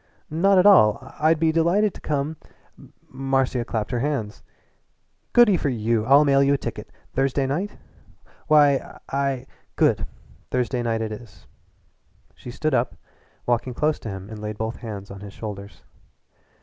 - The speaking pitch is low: Yes, low, 130 Hz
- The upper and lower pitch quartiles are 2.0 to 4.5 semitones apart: No, average, 5.3 semitones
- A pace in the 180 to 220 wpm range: No, average, 155 wpm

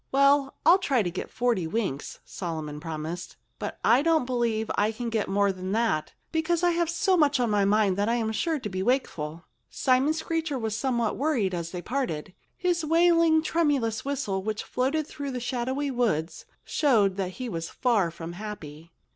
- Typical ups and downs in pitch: No, wide, 6.9 semitones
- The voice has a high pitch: Yes, high, 235 Hz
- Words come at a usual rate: Yes, average, 180 wpm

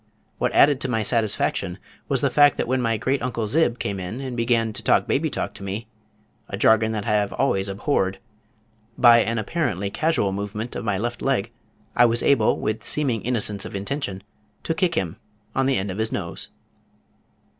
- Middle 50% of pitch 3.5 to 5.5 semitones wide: Yes, average, 4.4 semitones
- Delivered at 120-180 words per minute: No, average, 195 wpm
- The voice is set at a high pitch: No, low, 115 Hz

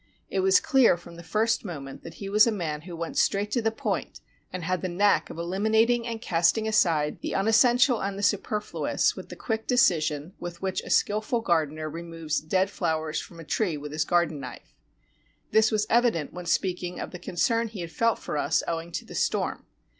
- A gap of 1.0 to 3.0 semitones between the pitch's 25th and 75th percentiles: No, average, 4.8 semitones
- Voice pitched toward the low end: No, medium, 185 Hz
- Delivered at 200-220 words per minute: Yes, fast, 205 wpm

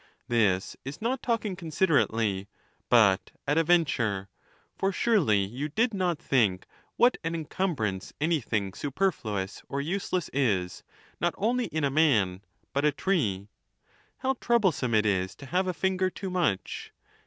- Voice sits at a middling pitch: Yes, medium, 145 Hz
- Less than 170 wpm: Yes, average, 140 wpm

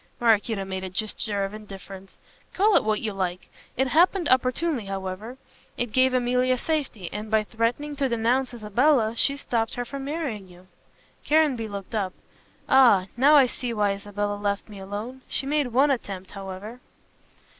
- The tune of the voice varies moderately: Yes, average, 4.6 semitones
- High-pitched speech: Yes, high, 225 Hz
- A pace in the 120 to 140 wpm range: No, average, 165 wpm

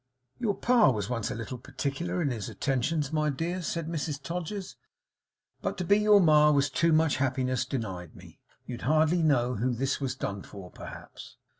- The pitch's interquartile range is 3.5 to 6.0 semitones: Yes, average, 4.9 semitones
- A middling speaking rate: Yes, average, 180 wpm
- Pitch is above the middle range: No, medium, 145 Hz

